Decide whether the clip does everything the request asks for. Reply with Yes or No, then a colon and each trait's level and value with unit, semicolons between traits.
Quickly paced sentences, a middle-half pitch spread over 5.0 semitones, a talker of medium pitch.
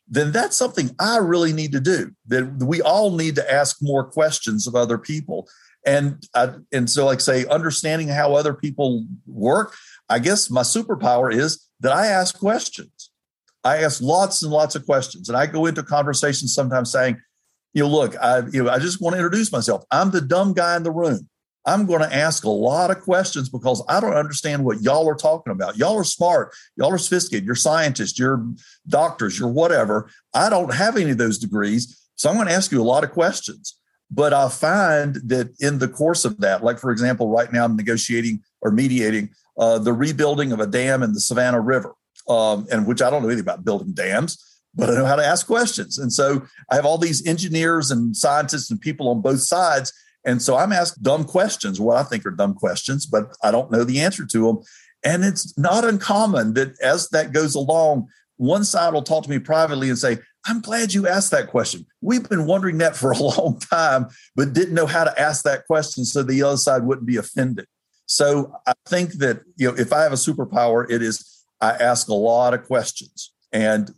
Yes: fast, 215 wpm; wide, 5.5 semitones; medium, 145 Hz